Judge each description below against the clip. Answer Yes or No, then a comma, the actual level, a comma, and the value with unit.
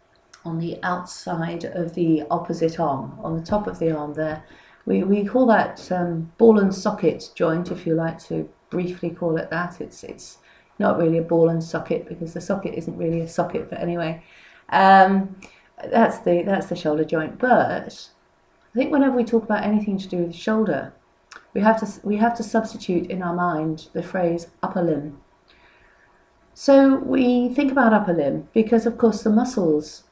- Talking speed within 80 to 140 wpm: No, average, 185 wpm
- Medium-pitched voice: Yes, medium, 175 Hz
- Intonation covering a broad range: No, average, 4.5 semitones